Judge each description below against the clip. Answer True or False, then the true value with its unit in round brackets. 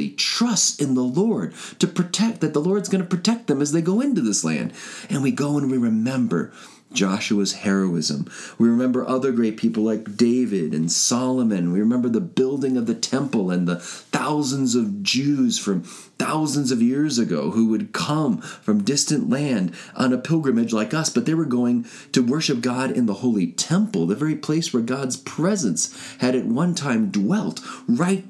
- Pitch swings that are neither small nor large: False (7.8 semitones)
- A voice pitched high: False (140 Hz)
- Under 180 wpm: False (185 wpm)